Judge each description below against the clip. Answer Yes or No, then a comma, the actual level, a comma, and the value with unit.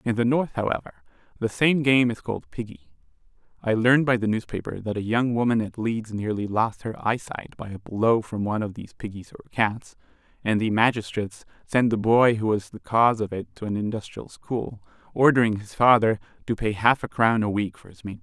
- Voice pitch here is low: Yes, low, 110 Hz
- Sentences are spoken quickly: Yes, fast, 215 wpm